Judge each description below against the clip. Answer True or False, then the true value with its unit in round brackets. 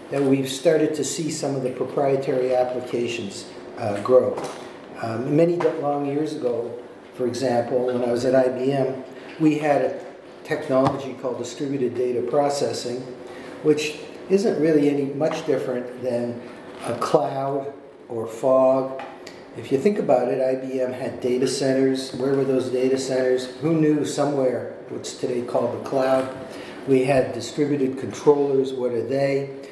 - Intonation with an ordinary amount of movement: False (2.0 semitones)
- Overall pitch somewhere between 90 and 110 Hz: False (130 Hz)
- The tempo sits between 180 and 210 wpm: False (145 wpm)